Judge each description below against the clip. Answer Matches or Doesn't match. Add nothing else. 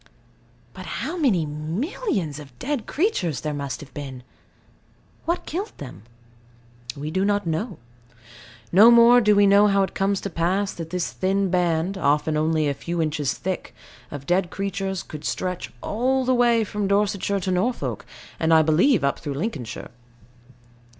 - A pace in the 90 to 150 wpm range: Doesn't match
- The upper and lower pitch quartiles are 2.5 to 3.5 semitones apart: Doesn't match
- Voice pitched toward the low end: Doesn't match